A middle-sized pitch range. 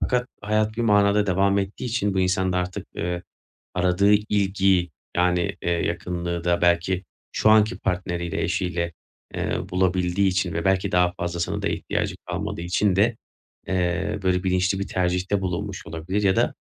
No: narrow, 2.2 semitones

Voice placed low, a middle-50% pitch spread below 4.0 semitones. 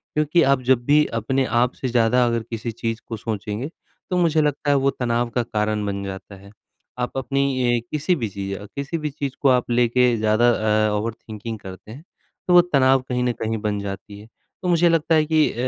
No: low, 120 Hz; average, 4.3 semitones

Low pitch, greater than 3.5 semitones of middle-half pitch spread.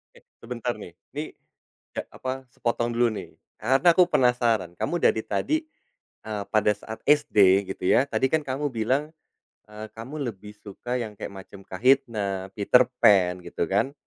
Yes: low, 115 Hz; average, 4.6 semitones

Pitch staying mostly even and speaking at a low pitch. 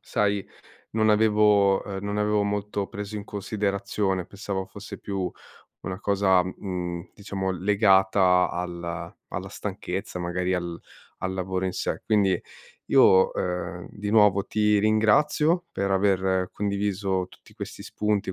Yes: narrow, 2.0 semitones; low, 100 Hz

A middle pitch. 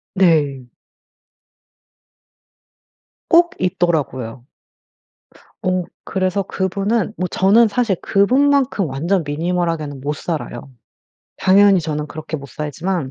Yes: medium, 180 Hz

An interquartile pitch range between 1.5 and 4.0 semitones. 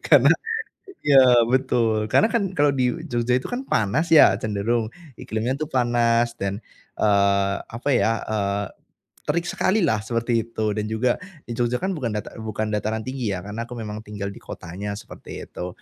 Yes: average, 3.2 semitones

